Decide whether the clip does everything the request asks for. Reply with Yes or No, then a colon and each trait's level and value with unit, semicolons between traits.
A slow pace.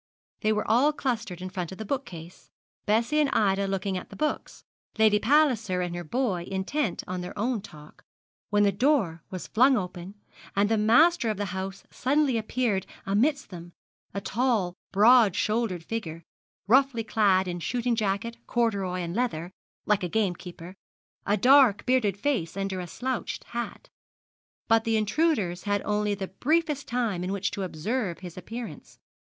No: average, 165 wpm